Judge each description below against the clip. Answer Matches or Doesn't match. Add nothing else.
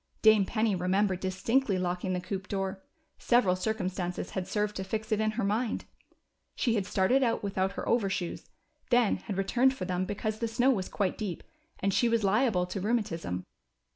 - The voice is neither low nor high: Doesn't match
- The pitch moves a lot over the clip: Doesn't match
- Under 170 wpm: Doesn't match